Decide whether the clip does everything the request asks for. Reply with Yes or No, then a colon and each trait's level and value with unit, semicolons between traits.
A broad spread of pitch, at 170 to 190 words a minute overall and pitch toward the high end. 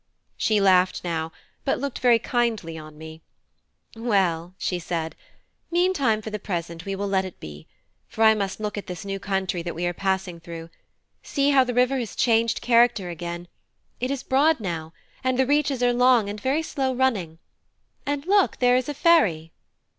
Yes: wide, 6.5 semitones; average, 185 wpm; high, 210 Hz